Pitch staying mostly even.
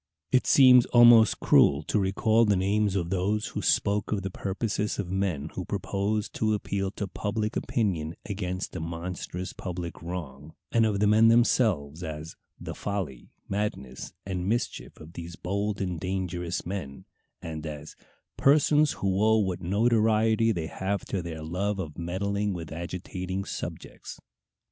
No: average, 3.7 semitones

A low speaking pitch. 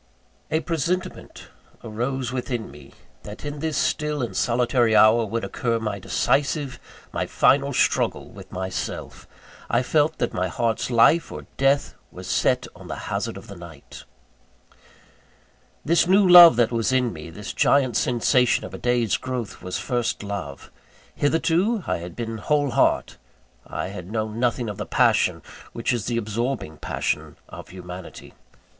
Yes: low, 120 Hz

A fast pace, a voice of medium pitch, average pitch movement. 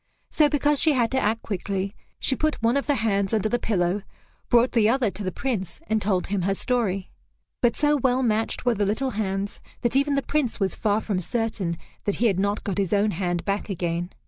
No: fast, 225 wpm; high, 215 Hz; average, 4.2 semitones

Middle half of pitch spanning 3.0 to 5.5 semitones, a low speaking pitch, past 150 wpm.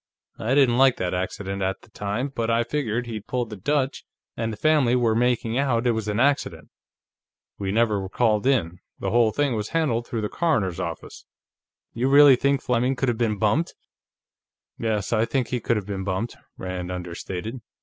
Yes: average, 3.8 semitones; low, 115 Hz; average, 190 wpm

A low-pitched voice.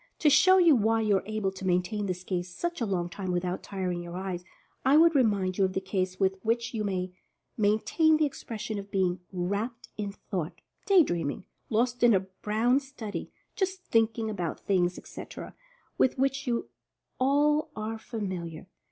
No: high, 210 Hz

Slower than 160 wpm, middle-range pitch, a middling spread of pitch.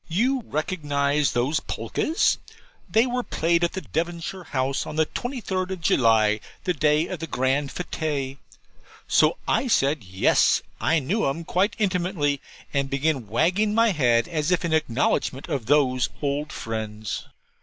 Yes: average, 145 wpm; medium, 155 Hz; average, 5.0 semitones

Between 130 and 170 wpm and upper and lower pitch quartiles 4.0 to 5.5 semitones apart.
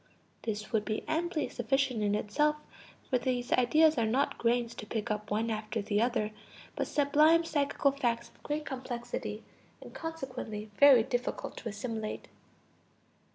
Yes: average, 150 wpm; average, 4.6 semitones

